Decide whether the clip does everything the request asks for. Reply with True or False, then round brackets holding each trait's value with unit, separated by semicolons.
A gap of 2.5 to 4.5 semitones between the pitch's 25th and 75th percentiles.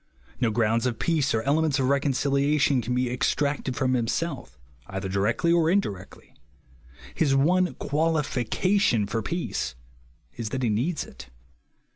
False (5.1 semitones)